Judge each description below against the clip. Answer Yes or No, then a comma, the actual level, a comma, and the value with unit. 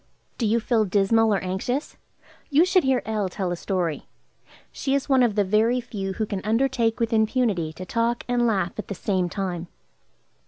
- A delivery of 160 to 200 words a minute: Yes, average, 190 wpm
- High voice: Yes, high, 220 Hz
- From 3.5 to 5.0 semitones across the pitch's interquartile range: Yes, average, 3.9 semitones